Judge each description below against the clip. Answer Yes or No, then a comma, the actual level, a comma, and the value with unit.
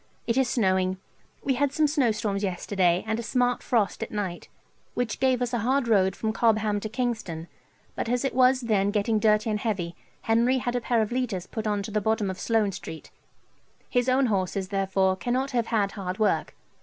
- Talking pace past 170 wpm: Yes, average, 200 wpm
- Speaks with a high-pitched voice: Yes, high, 220 Hz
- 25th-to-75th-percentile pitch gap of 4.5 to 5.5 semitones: No, average, 3.8 semitones